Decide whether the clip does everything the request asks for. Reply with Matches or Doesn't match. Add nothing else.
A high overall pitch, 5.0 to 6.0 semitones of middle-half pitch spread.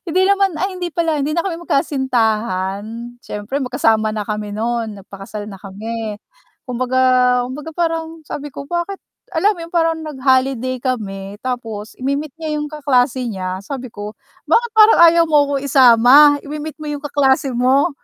Matches